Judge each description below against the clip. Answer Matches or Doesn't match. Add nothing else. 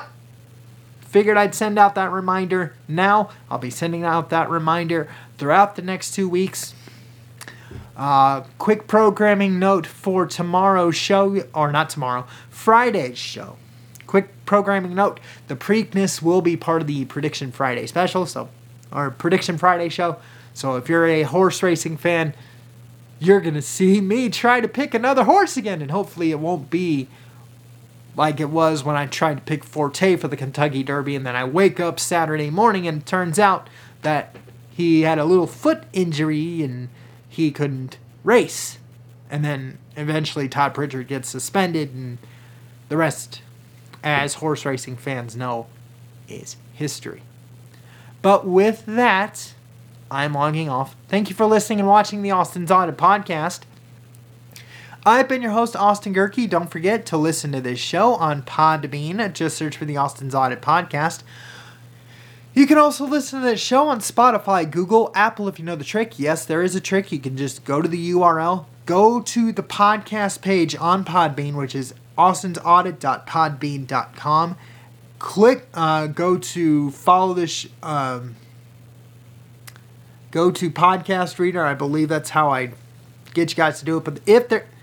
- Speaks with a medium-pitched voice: Matches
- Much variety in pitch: Matches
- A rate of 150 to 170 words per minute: Matches